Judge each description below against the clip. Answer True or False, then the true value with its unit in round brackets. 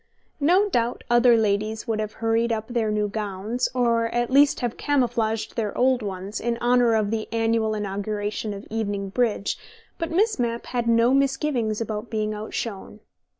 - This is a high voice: True (225 Hz)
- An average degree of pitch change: False (2.3 semitones)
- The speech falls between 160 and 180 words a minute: True (165 wpm)